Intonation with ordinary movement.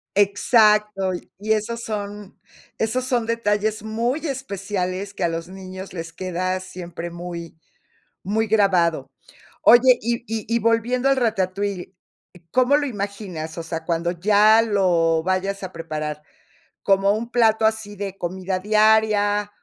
Yes: average, 3.1 semitones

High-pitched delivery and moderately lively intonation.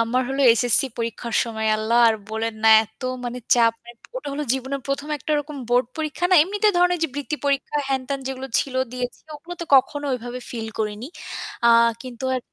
Yes: very high, 255 Hz; average, 3.6 semitones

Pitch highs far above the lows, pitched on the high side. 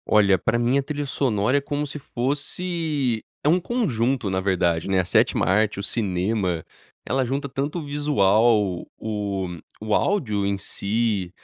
No: wide, 6.1 semitones; low, 115 Hz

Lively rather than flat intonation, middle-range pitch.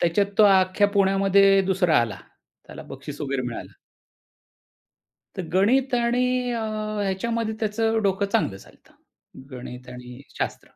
No: wide, 6.5 semitones; high, 195 Hz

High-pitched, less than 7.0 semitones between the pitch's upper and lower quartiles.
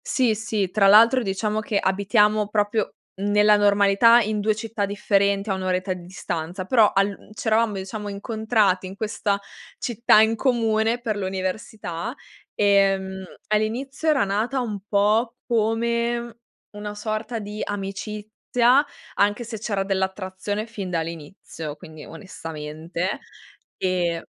Yes: high, 205 Hz; narrow, 2.4 semitones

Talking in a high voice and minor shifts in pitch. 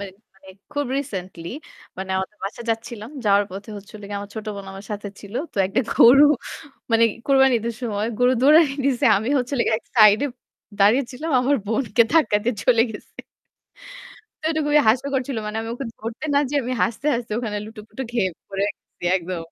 No: high, 225 Hz; average, 4.2 semitones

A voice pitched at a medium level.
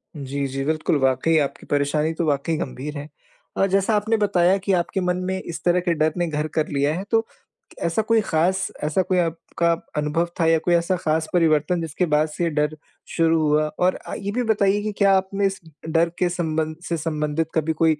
Yes: medium, 165 Hz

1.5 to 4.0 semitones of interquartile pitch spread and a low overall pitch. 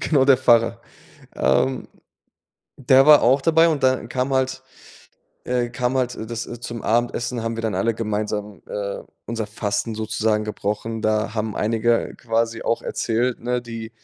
Yes: narrow, 2.5 semitones; low, 115 Hz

